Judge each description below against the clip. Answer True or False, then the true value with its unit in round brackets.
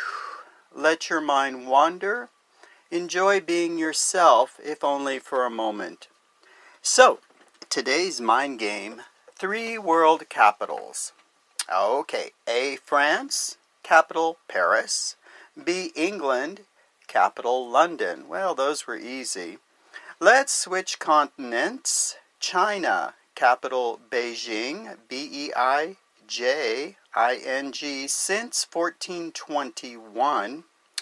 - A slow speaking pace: True (90 wpm)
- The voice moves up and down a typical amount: False (8.3 semitones)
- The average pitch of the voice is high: False (165 Hz)